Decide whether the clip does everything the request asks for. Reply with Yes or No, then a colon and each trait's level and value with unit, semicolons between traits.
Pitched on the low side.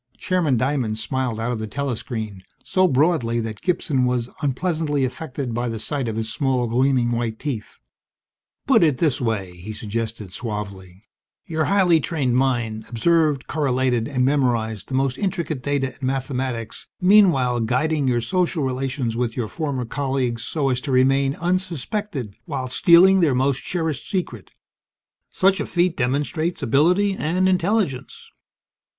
Yes: low, 130 Hz